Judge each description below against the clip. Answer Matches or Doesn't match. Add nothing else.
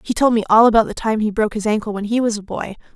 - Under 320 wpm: Doesn't match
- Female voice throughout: Matches